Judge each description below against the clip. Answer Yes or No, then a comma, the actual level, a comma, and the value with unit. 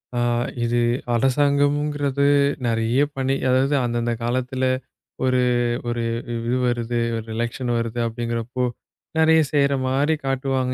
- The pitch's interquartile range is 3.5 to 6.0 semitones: No, average, 2.8 semitones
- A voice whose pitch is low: Yes, low, 130 Hz